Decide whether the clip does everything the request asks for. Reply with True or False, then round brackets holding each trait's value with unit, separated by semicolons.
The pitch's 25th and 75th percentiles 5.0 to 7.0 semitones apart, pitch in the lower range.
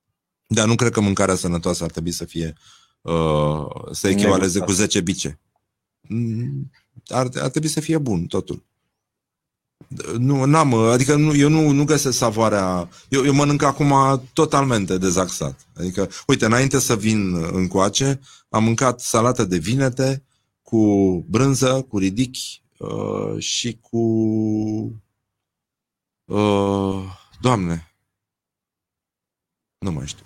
True (5.5 semitones; 110 Hz)